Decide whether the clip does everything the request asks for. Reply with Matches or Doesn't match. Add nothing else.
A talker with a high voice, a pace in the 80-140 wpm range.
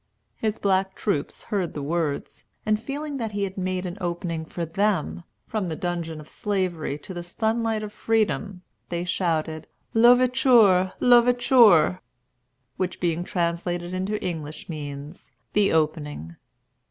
Doesn't match